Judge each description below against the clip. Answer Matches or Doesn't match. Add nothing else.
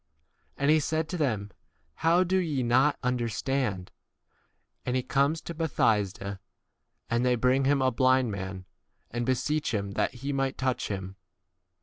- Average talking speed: Matches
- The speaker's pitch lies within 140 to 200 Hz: Doesn't match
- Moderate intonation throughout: Matches